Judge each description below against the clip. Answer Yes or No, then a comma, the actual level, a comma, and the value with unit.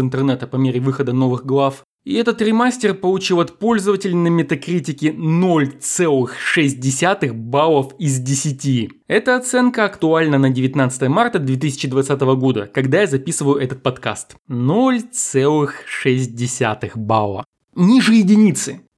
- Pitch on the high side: No, medium, 140 Hz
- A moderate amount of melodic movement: No, wide, 5.7 semitones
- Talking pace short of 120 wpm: Yes, slow, 110 wpm